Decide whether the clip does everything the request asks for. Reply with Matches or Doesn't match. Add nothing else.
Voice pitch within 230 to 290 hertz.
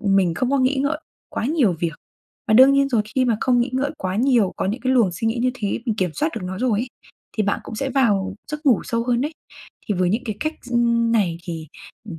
Matches